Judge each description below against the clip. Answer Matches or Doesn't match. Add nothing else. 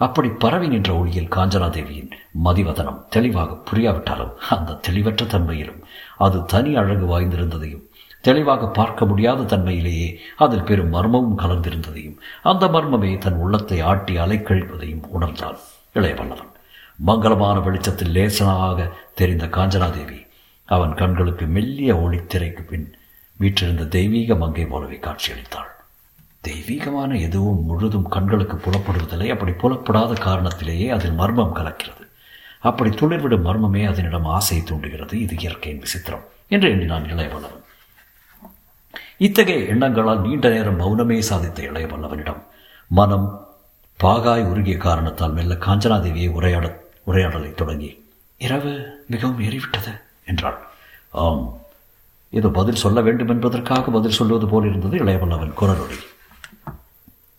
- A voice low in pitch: Matches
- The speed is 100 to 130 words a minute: Matches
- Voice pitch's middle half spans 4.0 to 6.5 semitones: Matches